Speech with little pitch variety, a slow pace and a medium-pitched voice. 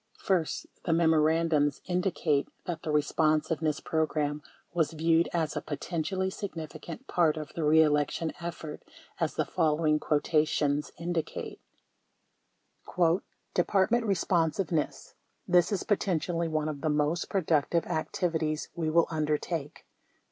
Yes: narrow, 2.1 semitones; slow, 120 wpm; medium, 160 Hz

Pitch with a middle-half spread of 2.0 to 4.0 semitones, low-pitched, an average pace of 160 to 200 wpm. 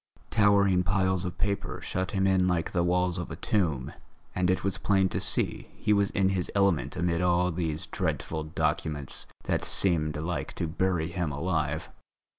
Yes: narrow, 2.4 semitones; very low, 90 Hz; average, 175 wpm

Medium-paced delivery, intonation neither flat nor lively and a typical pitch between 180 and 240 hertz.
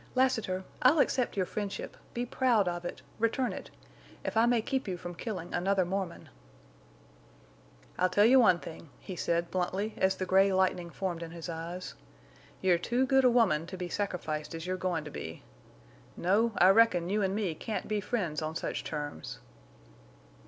Yes: average, 170 wpm; average, 4.2 semitones; medium, 185 Hz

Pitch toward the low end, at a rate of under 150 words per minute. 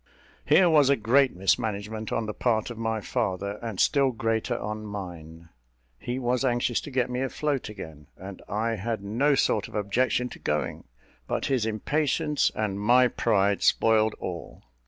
No: low, 110 Hz; average, 165 wpm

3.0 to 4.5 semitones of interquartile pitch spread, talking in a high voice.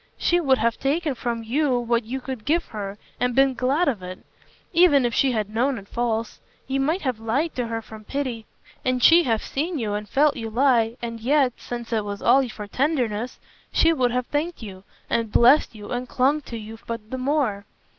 Yes: average, 3.6 semitones; high, 245 Hz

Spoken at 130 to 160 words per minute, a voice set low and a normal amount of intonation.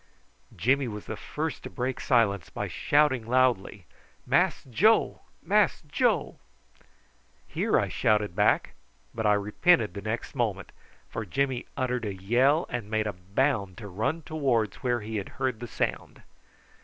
Yes: average, 150 wpm; low, 115 Hz; average, 4.3 semitones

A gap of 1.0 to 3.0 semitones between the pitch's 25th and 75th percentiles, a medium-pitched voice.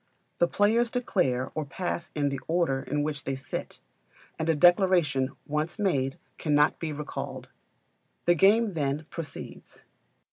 No: average, 3.8 semitones; medium, 155 Hz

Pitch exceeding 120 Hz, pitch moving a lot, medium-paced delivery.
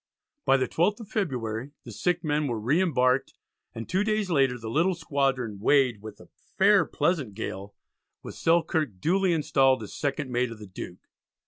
Yes: low, 135 Hz; wide, 6.5 semitones; average, 180 wpm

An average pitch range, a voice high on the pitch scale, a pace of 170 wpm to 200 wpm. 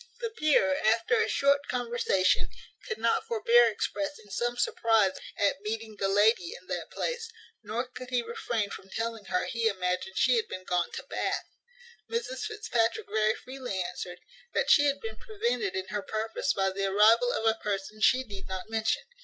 Yes: average, 4.7 semitones; high, 225 Hz; average, 180 wpm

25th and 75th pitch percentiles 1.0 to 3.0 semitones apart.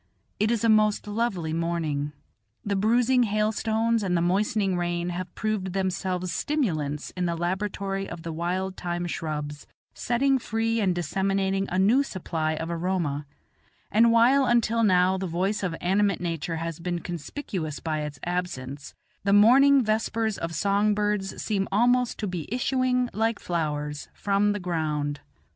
No: average, 4.2 semitones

